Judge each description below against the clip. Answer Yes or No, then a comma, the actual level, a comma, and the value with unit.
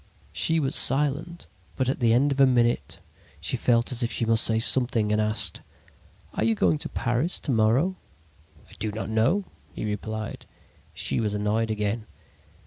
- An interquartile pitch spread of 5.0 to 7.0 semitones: No, average, 3.5 semitones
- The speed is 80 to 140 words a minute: No, average, 175 wpm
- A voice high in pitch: No, low, 115 Hz